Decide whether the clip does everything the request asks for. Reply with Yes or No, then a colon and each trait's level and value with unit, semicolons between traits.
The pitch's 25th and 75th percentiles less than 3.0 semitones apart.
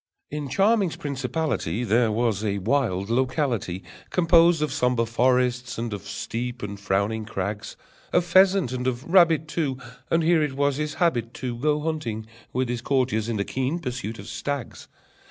No: average, 5.0 semitones